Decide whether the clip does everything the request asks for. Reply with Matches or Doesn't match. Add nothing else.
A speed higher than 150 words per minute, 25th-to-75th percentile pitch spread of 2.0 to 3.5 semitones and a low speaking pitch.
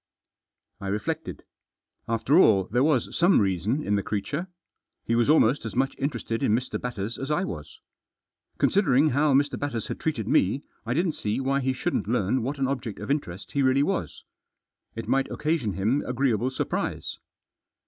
Doesn't match